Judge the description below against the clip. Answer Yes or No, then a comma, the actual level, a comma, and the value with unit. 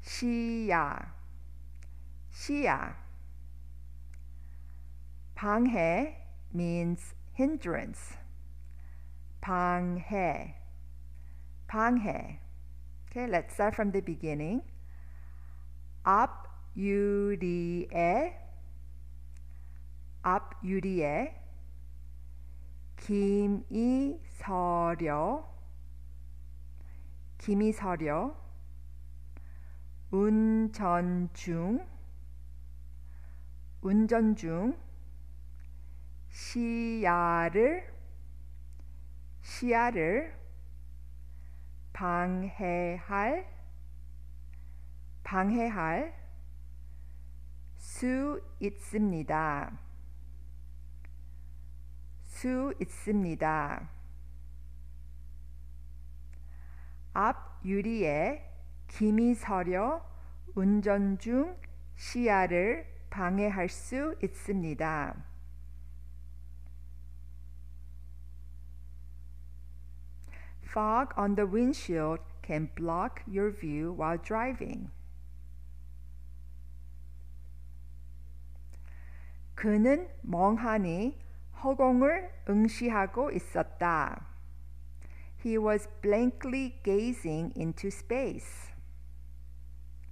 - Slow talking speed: Yes, slow, 45 wpm